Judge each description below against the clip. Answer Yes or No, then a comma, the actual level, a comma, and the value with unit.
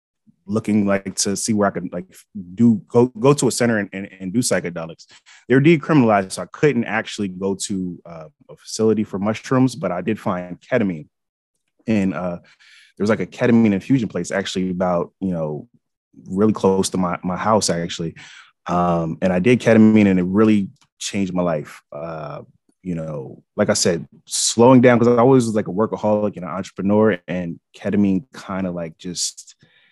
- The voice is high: No, low, 100 Hz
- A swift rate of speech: No, average, 185 wpm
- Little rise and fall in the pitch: No, average, 3.9 semitones